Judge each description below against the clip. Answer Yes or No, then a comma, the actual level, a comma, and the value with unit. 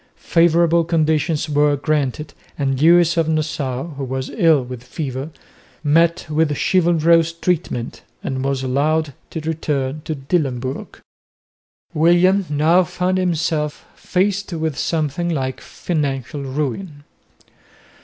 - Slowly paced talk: Yes, slow, 115 wpm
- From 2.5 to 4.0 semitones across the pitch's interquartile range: Yes, average, 3.4 semitones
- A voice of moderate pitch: Yes, medium, 155 Hz